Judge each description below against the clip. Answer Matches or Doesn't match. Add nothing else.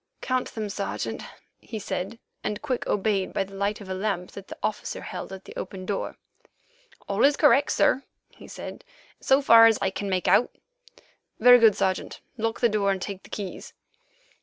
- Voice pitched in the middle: Doesn't match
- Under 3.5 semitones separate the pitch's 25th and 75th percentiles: Matches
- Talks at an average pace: Matches